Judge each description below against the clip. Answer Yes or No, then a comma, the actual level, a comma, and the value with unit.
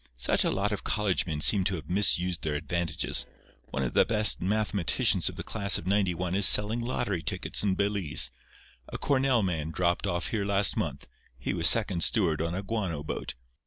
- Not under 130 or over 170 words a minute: No, average, 195 wpm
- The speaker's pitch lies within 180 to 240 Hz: No, very low, 95 Hz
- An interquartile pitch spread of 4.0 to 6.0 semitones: No, average, 3.5 semitones